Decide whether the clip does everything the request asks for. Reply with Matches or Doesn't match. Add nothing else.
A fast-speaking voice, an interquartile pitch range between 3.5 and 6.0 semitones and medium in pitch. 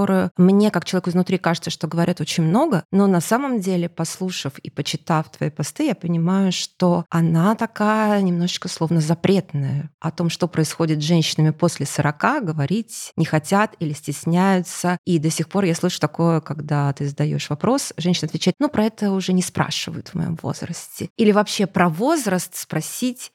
Doesn't match